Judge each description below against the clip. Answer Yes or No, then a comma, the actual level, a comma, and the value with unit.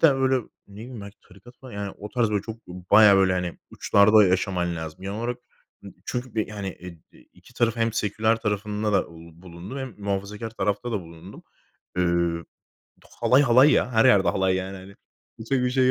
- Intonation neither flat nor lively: Yes, average, 3.7 semitones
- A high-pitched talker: No, low, 105 Hz